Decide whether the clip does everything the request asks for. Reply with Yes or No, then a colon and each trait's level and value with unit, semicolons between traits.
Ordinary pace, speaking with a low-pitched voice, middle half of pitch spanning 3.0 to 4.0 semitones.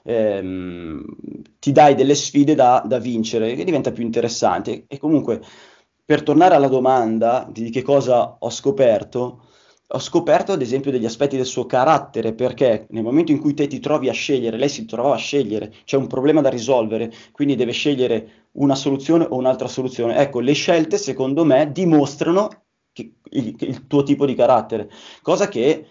No: fast, 175 wpm; low, 130 Hz; average, 3.6 semitones